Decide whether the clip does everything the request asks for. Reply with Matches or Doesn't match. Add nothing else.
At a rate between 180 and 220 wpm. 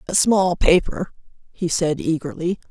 Doesn't match